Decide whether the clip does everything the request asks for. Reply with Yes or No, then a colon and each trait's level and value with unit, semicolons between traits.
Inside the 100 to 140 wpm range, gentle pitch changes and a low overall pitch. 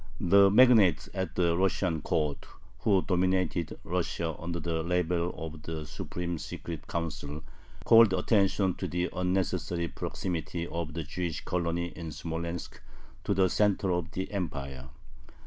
Yes: slow, 135 wpm; narrow, 2.3 semitones; very low, 85 Hz